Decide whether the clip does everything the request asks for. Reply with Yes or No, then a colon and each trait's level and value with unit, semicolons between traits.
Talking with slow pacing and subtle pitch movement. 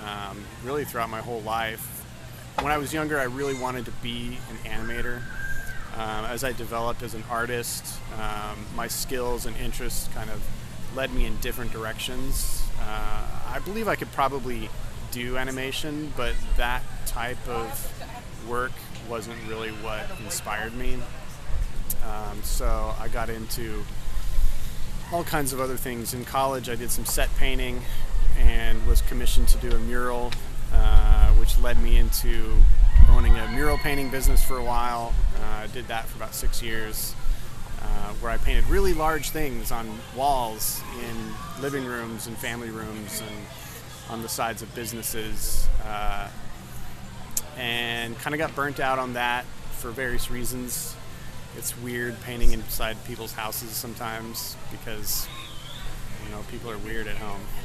No: average, 155 wpm; narrow, 2.2 semitones